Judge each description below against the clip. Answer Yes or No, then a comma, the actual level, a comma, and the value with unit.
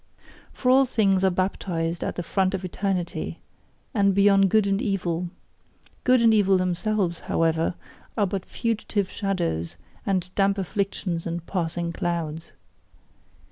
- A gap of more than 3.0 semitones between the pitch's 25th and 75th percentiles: No, average, 2.7 semitones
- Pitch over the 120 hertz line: Yes, high, 190 Hz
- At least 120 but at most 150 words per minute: Yes, slow, 135 wpm